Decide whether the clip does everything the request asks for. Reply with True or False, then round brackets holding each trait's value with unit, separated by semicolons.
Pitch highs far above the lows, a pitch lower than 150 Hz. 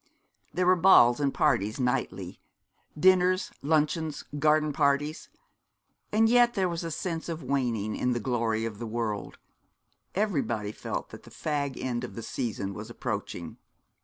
True (6.0 semitones; 140 Hz)